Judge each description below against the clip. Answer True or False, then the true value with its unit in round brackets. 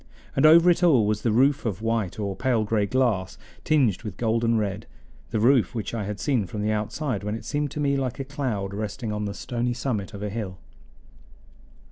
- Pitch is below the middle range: True (115 Hz)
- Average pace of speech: False (210 wpm)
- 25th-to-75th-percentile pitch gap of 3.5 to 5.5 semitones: True (4.1 semitones)